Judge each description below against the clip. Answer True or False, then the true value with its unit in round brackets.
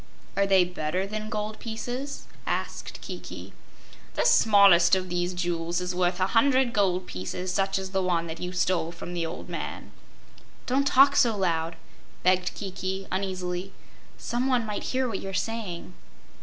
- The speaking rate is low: False (155 wpm)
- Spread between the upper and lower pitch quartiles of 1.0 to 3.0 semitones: False (3.4 semitones)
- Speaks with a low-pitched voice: False (190 Hz)